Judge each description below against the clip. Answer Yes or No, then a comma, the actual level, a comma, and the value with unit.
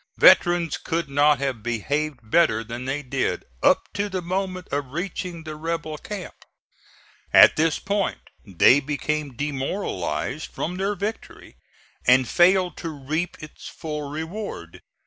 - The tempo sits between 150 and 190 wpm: No, slow, 135 wpm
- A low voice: No, medium, 155 Hz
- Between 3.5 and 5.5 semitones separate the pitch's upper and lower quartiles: Yes, average, 4.6 semitones